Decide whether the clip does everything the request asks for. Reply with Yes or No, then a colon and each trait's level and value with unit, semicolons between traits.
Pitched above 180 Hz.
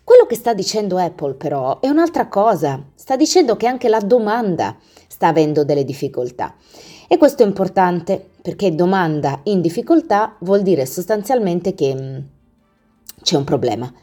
Yes: high, 190 Hz